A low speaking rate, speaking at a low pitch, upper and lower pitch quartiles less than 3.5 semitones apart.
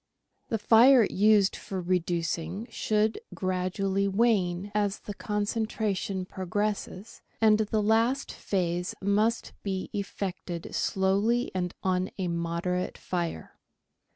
No: slow, 110 wpm; high, 195 Hz; average, 2.8 semitones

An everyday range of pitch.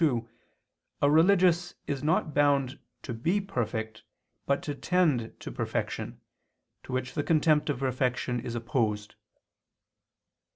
Yes: average, 4.6 semitones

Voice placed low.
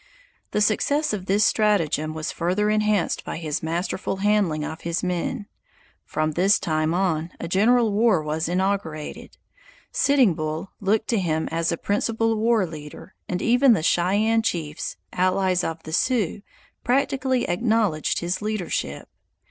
No: high, 190 Hz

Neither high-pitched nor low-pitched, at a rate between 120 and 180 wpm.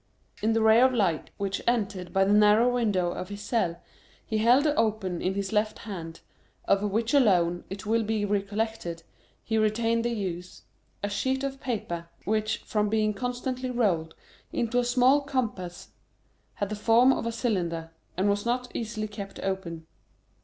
No: high, 215 Hz; average, 165 wpm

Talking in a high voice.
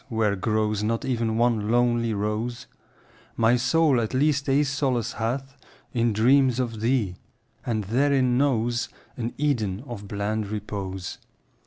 No: low, 115 Hz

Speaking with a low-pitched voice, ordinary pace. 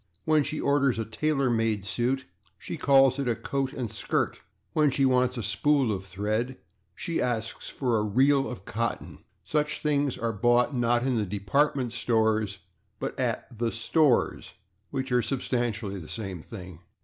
Yes: low, 120 Hz; average, 165 wpm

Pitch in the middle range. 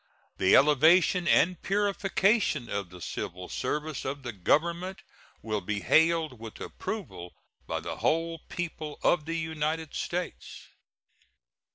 Yes: medium, 160 Hz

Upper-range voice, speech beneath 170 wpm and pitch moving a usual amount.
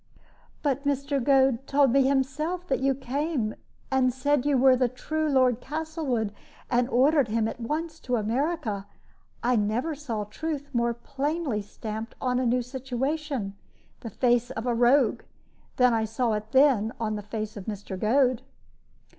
Yes: very high, 255 Hz; average, 160 wpm; average, 3.7 semitones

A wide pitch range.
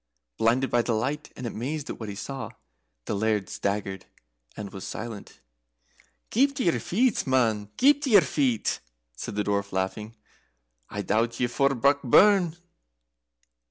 Yes: wide, 5.8 semitones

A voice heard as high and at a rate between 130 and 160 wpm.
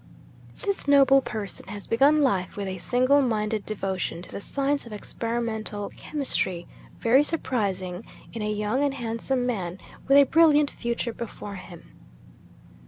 Yes: high, 230 Hz; average, 145 wpm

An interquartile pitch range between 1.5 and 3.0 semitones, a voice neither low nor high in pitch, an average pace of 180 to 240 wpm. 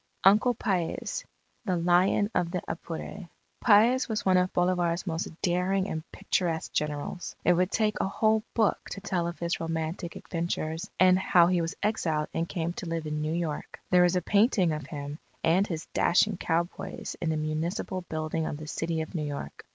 Yes: average, 2.7 semitones; medium, 175 Hz; average, 190 wpm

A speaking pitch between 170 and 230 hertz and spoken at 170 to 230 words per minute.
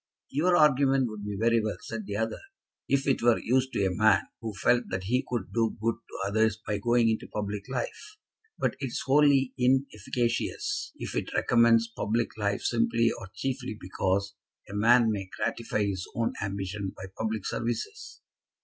No: low, 115 Hz; average, 175 wpm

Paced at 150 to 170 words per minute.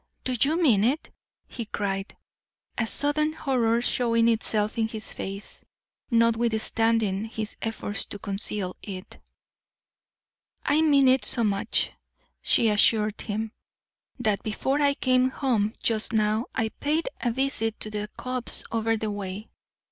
No: slow, 135 wpm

